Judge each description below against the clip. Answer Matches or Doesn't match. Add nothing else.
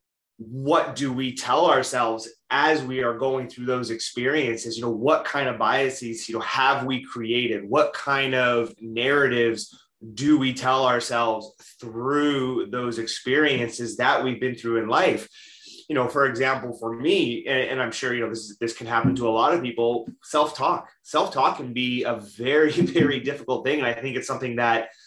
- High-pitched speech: Doesn't match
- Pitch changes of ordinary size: Doesn't match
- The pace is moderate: Matches